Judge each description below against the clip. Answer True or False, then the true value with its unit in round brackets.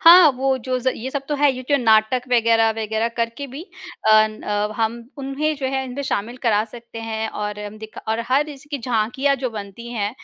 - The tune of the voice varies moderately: True (3.6 semitones)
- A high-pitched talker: True (235 Hz)